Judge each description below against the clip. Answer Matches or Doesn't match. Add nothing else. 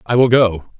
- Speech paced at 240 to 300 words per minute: Doesn't match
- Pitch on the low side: Matches